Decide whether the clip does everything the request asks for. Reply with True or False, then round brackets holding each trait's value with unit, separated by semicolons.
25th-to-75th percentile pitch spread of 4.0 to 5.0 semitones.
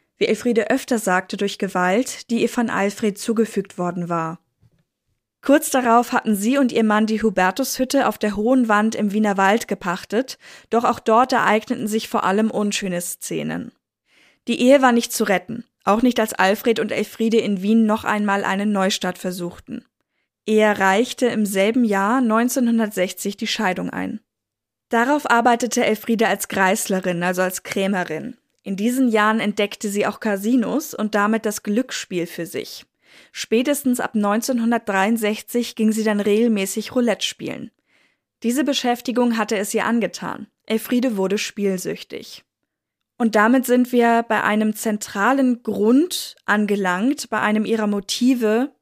False (3.0 semitones)